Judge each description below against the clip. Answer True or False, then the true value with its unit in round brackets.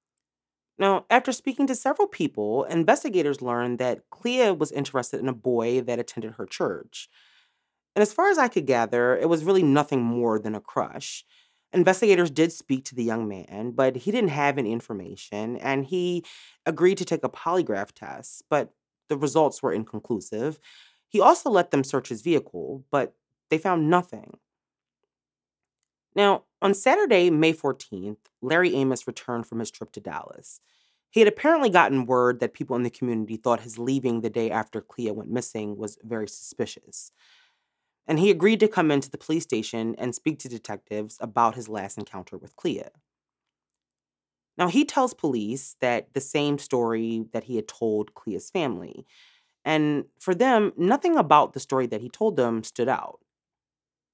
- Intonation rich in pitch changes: True (7.6 semitones)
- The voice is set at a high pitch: False (135 Hz)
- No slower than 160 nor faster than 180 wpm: True (170 wpm)